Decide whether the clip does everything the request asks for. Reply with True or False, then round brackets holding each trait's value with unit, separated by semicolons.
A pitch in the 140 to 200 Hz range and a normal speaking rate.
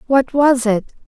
False (255 Hz; 160 wpm)